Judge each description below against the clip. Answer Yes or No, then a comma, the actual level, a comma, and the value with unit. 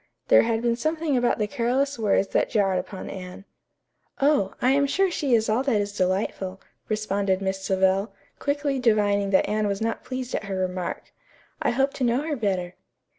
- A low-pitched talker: No, high, 215 Hz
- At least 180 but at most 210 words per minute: Yes, average, 185 wpm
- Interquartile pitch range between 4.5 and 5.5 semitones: Yes, average, 5.1 semitones